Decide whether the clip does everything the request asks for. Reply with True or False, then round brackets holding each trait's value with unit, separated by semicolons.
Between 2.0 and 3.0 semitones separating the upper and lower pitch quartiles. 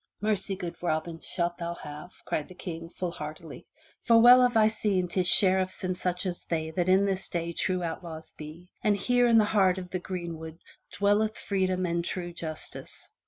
True (2.7 semitones)